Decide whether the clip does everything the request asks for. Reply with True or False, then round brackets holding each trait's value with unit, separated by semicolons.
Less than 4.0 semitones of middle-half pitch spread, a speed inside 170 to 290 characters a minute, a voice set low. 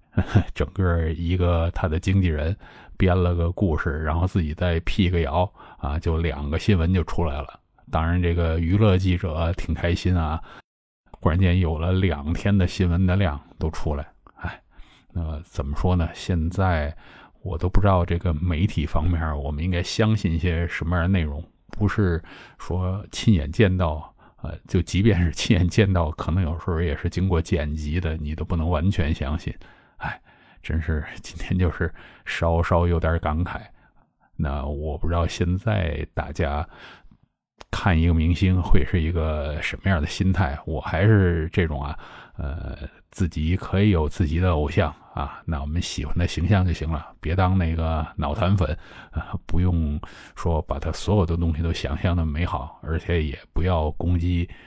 True (2.6 semitones; 245 characters per minute; 85 Hz)